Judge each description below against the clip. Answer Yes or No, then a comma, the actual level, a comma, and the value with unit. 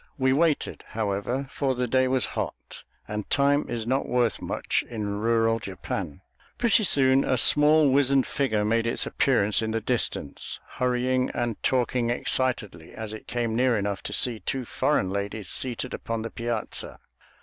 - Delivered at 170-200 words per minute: No, average, 160 wpm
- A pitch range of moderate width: Yes, average, 3.2 semitones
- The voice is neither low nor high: No, low, 120 Hz